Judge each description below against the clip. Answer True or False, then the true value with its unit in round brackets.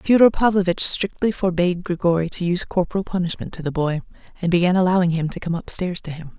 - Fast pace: False (195 wpm)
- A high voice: False (180 Hz)